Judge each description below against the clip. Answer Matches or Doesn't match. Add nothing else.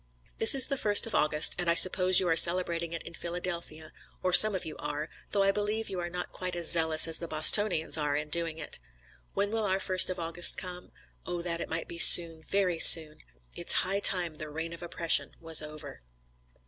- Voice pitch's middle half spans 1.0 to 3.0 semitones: Matches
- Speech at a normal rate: Doesn't match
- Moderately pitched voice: Matches